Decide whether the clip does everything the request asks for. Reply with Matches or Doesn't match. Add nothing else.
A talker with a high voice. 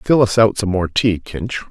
Doesn't match